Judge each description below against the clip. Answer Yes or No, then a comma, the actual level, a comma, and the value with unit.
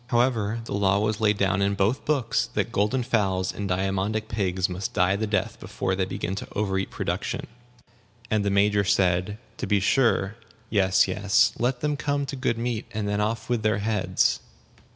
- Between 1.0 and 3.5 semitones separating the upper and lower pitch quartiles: Yes, average, 3.0 semitones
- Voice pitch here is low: Yes, low, 105 Hz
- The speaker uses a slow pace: No, average, 185 wpm